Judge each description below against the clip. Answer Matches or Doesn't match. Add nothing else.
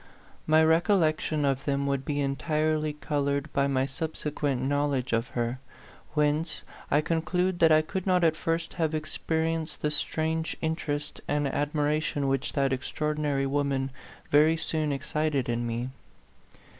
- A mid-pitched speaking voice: Matches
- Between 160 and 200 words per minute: Doesn't match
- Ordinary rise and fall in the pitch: Doesn't match